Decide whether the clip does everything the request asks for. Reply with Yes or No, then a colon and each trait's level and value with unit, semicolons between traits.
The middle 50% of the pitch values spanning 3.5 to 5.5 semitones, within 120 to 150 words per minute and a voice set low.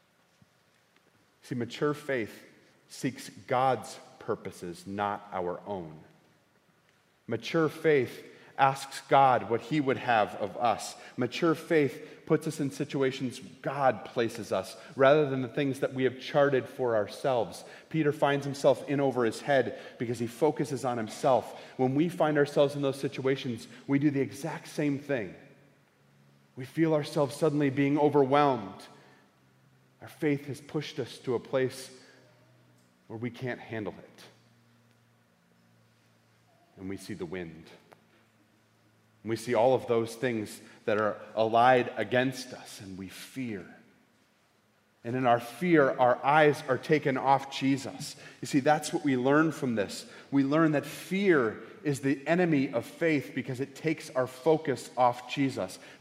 Yes: average, 4.1 semitones; average, 145 wpm; low, 130 Hz